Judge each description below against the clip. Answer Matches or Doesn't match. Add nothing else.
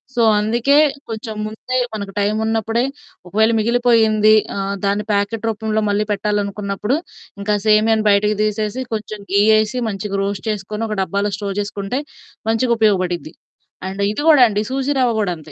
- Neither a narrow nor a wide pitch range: Doesn't match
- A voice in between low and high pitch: Doesn't match